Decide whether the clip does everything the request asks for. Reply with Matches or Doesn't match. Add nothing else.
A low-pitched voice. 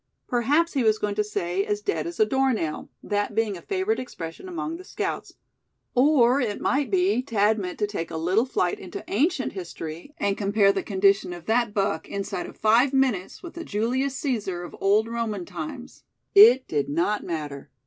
Doesn't match